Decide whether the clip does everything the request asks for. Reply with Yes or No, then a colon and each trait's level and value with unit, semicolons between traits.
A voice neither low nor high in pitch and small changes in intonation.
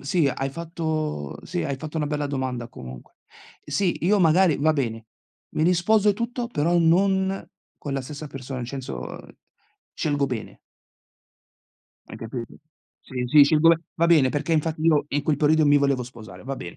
No: medium, 150 Hz; average, 4.0 semitones